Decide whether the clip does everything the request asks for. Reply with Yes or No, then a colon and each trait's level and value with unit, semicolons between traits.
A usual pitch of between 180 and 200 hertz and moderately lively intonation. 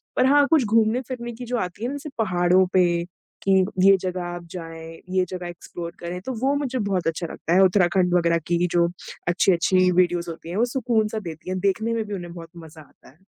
Yes: medium, 185 Hz; average, 4.3 semitones